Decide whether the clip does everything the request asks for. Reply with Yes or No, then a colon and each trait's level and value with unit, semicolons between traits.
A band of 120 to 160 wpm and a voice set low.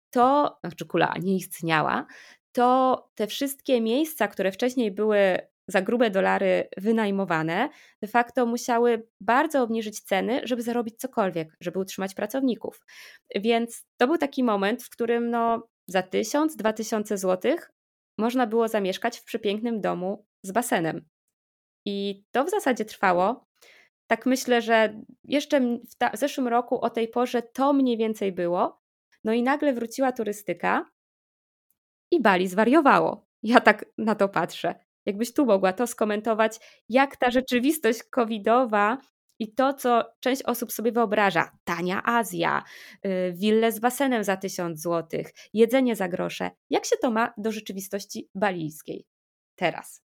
No: average, 140 wpm; high, 225 Hz